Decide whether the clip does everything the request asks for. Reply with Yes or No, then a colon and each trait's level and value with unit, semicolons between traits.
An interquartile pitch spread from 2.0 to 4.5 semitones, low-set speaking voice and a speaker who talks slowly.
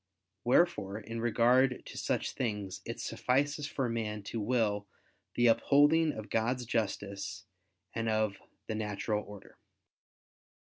Yes: average, 3.3 semitones; low, 115 Hz; slow, 125 wpm